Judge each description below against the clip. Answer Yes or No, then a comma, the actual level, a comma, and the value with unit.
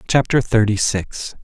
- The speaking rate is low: Yes, slow, 125 wpm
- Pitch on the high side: No, low, 110 Hz